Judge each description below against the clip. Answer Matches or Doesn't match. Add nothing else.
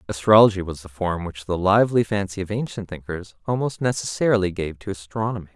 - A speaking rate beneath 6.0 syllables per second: Doesn't match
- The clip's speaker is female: Doesn't match